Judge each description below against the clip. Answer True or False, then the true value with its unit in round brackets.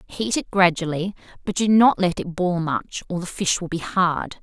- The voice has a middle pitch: True (180 Hz)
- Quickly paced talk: True (215 wpm)